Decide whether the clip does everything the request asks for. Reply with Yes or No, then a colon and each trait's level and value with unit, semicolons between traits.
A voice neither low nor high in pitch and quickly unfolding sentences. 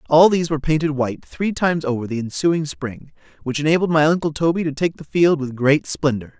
Yes: medium, 150 Hz; fast, 215 wpm